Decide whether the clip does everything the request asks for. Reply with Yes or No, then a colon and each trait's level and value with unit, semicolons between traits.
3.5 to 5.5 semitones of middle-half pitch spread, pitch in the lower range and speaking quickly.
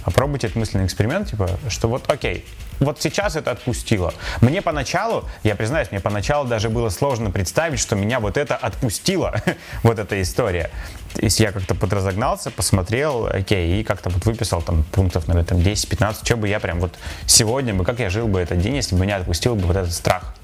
Yes: average, 3.9 semitones; low, 105 Hz; fast, 195 wpm